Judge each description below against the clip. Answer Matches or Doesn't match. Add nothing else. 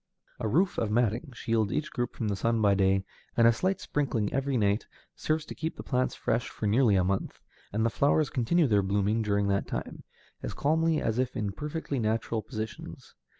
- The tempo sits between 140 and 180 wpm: Doesn't match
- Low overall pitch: Matches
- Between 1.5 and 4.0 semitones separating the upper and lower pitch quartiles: Doesn't match